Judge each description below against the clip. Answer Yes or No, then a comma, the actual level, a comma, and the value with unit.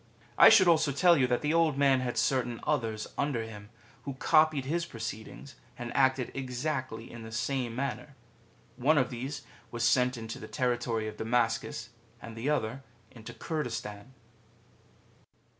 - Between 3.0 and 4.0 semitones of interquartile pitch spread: Yes, average, 3.5 semitones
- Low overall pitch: Yes, low, 125 Hz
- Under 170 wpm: Yes, average, 160 wpm